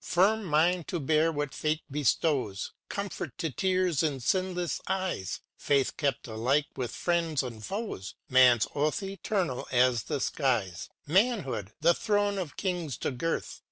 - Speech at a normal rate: Yes, average, 150 wpm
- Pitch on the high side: No, medium, 155 Hz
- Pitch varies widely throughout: Yes, wide, 6.1 semitones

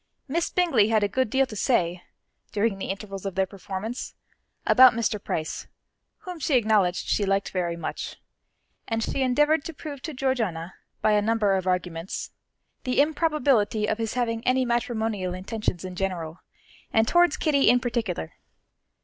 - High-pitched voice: Yes, high, 220 Hz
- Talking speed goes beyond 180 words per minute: No, average, 160 wpm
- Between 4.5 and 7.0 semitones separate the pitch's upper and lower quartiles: Yes, average, 5.2 semitones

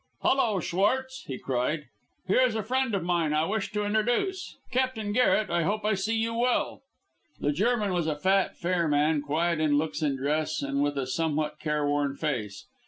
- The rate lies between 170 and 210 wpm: Yes, average, 185 wpm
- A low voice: No, medium, 170 Hz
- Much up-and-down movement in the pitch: Yes, wide, 6.5 semitones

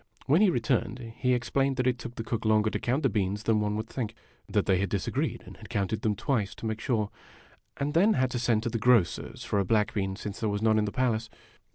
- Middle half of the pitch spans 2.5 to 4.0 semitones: Yes, average, 3.0 semitones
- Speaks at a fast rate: Yes, fast, 255 wpm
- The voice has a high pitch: No, low, 110 Hz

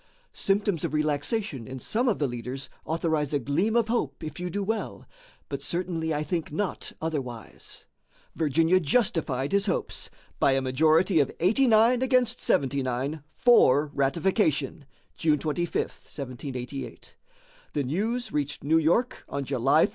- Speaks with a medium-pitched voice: Yes, medium, 155 Hz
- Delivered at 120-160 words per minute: Yes, average, 140 wpm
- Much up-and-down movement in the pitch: Yes, wide, 6.0 semitones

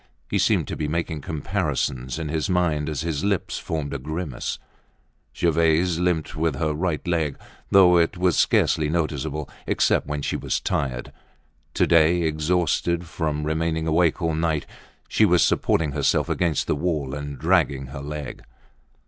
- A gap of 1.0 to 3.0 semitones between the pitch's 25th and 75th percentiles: Yes, narrow, 2.5 semitones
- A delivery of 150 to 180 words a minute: Yes, average, 155 wpm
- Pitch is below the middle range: Yes, very low, 80 Hz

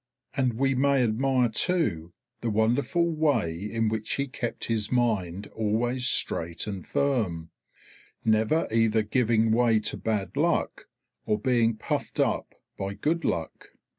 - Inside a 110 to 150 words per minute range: Yes, slow, 135 wpm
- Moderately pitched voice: No, low, 115 Hz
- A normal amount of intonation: Yes, average, 3.3 semitones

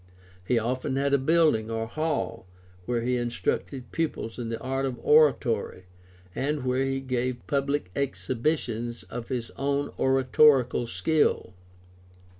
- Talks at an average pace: No, slow, 130 wpm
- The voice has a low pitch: Yes, low, 130 Hz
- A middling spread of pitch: Yes, average, 3.1 semitones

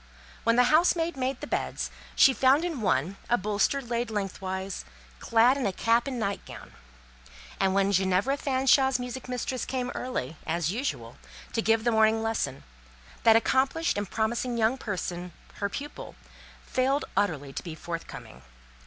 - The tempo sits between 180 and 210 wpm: No, average, 155 wpm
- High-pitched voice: Yes, high, 230 Hz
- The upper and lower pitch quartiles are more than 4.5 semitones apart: Yes, average, 5.1 semitones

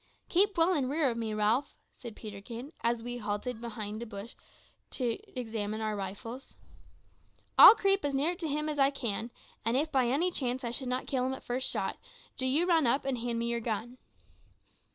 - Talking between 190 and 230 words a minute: Yes, fast, 205 wpm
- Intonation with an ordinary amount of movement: Yes, average, 3.8 semitones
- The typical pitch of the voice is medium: No, high, 245 Hz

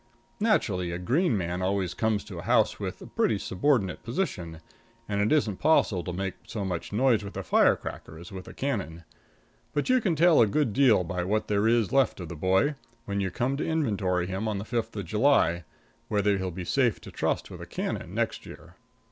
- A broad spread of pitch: Yes, wide, 5.7 semitones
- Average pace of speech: No, fast, 210 wpm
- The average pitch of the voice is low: Yes, low, 100 Hz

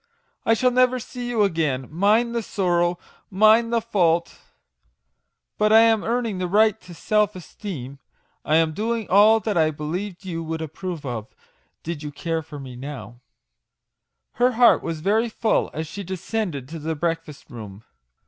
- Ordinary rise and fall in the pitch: No, wide, 5.9 semitones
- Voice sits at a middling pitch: Yes, medium, 180 Hz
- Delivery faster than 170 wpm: No, average, 165 wpm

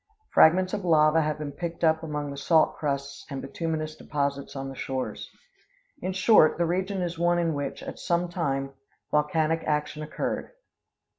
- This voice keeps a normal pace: Yes, average, 165 wpm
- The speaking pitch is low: No, medium, 155 Hz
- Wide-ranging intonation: No, average, 3.1 semitones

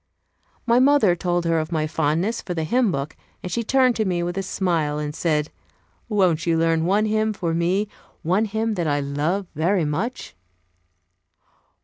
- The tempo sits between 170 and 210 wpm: Yes, average, 175 wpm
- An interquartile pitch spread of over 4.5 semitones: Yes, average, 4.9 semitones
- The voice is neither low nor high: Yes, medium, 175 Hz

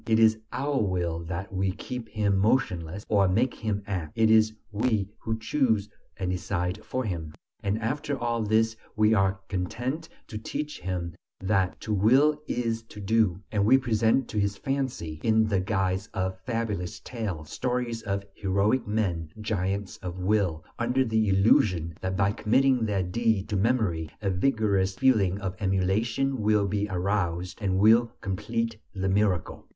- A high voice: No, low, 105 Hz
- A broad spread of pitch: No, average, 3.2 semitones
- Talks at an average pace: Yes, average, 170 wpm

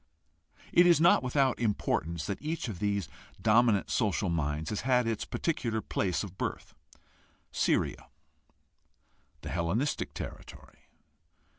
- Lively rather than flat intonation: Yes, wide, 5.8 semitones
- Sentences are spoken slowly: Yes, slow, 120 wpm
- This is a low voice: Yes, low, 110 Hz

